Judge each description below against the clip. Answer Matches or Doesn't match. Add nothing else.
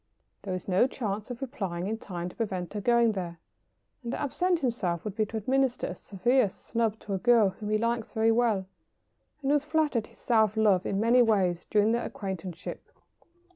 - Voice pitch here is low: Doesn't match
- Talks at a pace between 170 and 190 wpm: Doesn't match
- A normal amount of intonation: Matches